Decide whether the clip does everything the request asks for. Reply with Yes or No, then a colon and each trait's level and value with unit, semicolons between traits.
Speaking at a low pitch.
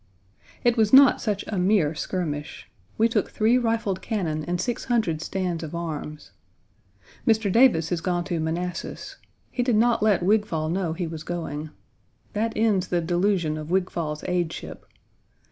No: medium, 180 Hz